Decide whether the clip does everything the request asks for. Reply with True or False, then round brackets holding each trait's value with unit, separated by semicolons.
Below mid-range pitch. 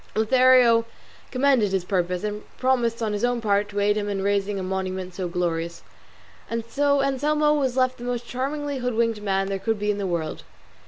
False (215 Hz)